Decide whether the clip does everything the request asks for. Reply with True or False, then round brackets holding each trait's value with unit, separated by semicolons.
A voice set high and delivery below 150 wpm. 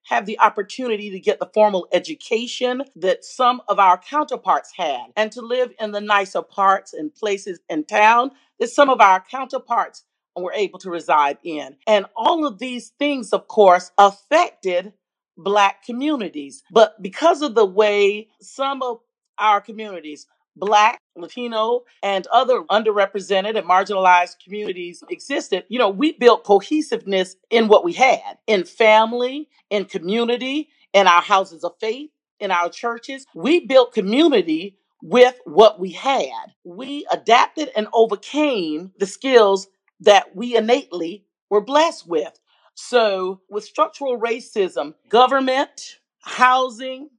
True (220 Hz; 140 wpm)